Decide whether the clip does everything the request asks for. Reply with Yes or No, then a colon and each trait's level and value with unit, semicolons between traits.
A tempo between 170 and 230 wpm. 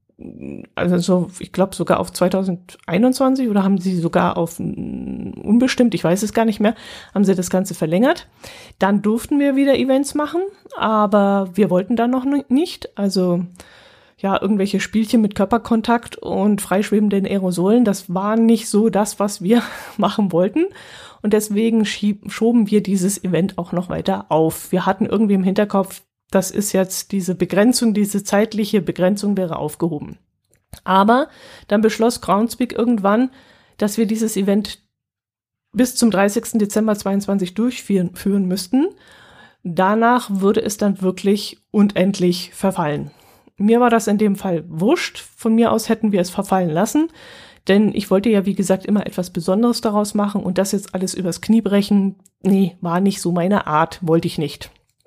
No: average, 160 wpm